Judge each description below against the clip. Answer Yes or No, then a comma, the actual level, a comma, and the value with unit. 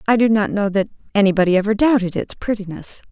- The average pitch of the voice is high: Yes, high, 205 Hz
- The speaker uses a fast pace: No, average, 195 wpm